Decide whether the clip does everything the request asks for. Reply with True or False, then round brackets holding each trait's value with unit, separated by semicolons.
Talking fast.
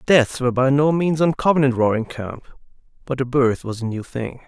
True (215 wpm)